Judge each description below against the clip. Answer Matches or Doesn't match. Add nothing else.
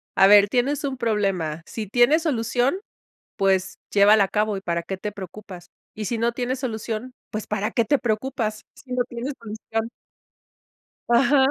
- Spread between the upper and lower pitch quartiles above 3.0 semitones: Matches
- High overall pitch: Matches